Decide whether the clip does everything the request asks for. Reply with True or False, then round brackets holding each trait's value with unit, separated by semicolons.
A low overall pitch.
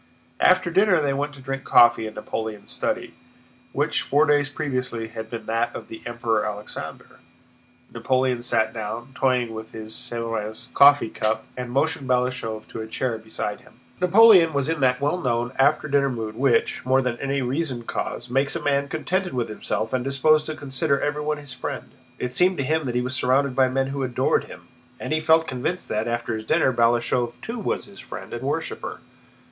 True (130 Hz)